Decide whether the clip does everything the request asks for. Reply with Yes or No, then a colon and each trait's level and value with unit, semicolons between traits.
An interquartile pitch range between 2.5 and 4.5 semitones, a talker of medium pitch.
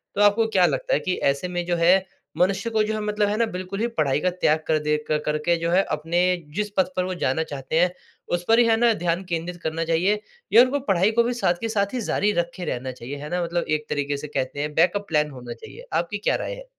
No: average, 5.2 semitones; medium, 175 Hz